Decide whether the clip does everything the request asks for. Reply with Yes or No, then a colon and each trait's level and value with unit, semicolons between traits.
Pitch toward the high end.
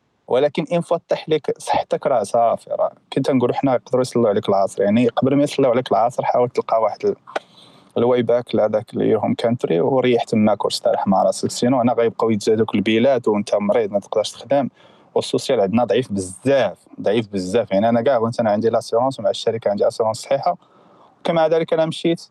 No: low, 125 Hz